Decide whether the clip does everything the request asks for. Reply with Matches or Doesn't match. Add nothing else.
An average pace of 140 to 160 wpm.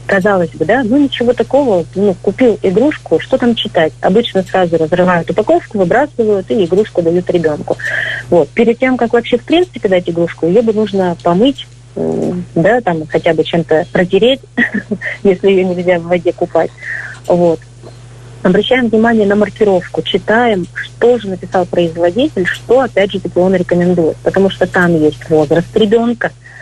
Matches